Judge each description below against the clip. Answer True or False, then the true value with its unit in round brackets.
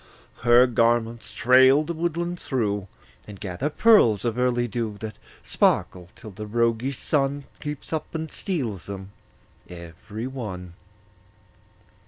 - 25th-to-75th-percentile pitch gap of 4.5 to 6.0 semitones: True (5.0 semitones)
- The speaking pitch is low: True (120 Hz)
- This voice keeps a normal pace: False (125 wpm)